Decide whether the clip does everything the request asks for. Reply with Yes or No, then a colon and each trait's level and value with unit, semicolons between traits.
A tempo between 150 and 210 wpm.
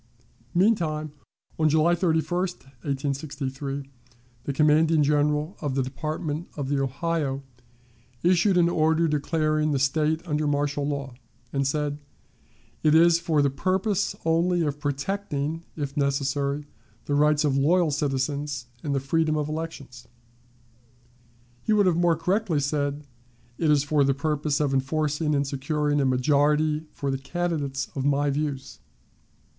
No: average, 140 wpm